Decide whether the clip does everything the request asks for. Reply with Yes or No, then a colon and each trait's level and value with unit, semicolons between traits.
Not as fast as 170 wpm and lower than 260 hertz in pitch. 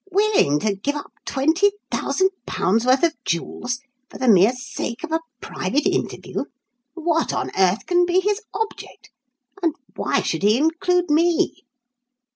No: average, 140 wpm; very high, 305 Hz